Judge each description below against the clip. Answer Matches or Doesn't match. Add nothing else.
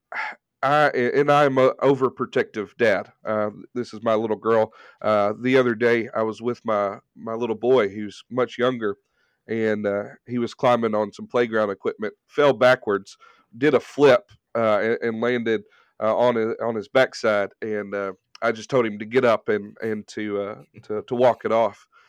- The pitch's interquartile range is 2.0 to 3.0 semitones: Matches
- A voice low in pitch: Matches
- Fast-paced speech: Doesn't match